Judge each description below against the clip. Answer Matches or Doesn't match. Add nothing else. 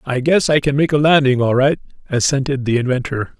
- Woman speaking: Doesn't match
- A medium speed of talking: Doesn't match